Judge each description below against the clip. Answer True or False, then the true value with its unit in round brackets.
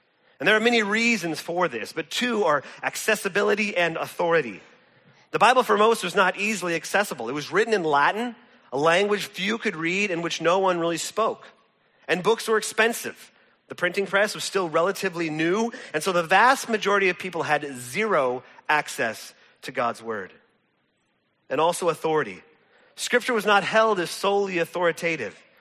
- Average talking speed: True (165 wpm)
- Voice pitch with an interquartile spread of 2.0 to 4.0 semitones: False (4.6 semitones)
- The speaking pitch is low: False (190 Hz)